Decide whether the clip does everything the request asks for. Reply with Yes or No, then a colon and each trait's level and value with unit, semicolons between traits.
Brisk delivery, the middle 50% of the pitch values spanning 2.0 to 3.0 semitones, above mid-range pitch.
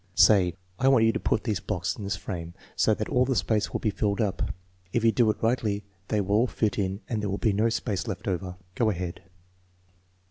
No: fast, 235 wpm; average, 2.7 semitones; low, 105 Hz